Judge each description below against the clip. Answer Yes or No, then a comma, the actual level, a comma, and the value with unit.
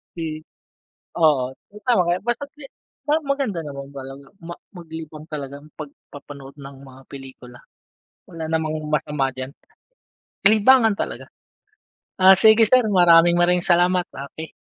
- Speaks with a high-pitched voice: No, medium, 165 Hz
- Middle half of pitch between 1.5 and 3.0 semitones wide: No, average, 5.1 semitones